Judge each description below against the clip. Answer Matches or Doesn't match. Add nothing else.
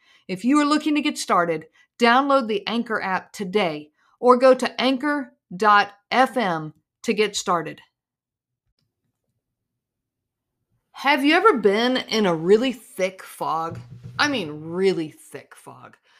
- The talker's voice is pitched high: Matches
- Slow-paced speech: Matches